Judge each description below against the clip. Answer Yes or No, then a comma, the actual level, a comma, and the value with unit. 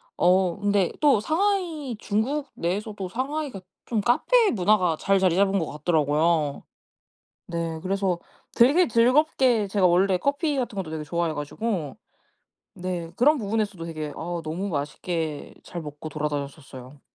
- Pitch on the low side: No, high, 190 Hz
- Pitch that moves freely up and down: Yes, wide, 6.2 semitones